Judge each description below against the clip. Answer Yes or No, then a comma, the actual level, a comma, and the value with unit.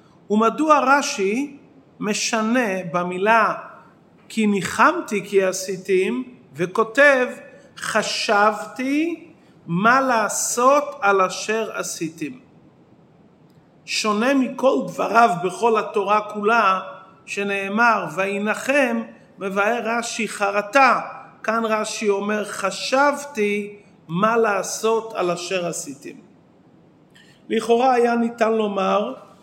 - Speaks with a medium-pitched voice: No, high, 215 Hz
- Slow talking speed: Yes, slow, 80 wpm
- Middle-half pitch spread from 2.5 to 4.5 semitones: Yes, average, 3.3 semitones